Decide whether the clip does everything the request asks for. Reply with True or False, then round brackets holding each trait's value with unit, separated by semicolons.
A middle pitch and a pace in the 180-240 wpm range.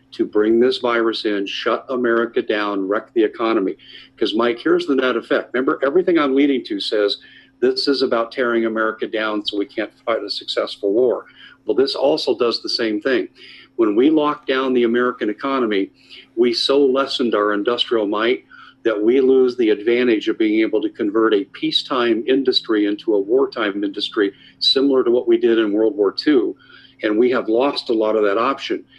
True (175 Hz; 190 wpm)